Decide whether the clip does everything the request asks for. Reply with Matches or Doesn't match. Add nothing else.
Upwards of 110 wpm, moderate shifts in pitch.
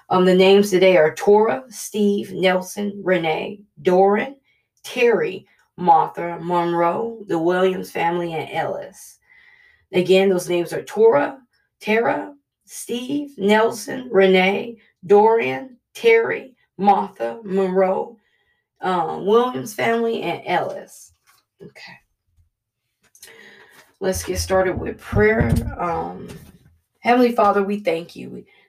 Doesn't match